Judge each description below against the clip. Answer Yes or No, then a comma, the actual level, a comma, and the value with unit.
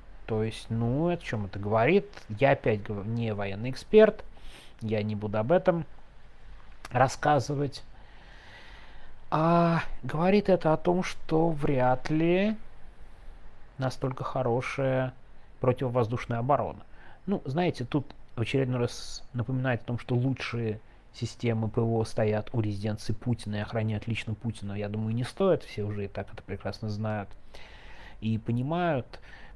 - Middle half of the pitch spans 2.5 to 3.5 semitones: No, average, 4.2 semitones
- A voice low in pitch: Yes, low, 120 Hz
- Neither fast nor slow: Yes, average, 130 wpm